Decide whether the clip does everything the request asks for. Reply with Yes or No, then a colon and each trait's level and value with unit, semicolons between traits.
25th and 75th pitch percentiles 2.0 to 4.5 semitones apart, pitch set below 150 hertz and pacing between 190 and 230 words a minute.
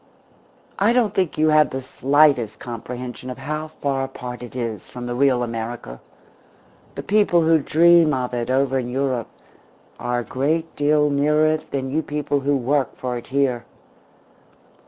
No: average, 3.6 semitones; low, 135 Hz; average, 165 wpm